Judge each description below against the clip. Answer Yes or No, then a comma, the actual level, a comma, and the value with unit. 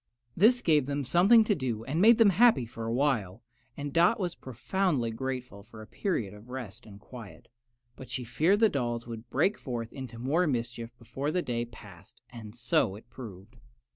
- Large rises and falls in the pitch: Yes, wide, 5.8 semitones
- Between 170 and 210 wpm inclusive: Yes, average, 190 wpm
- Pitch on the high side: No, low, 125 Hz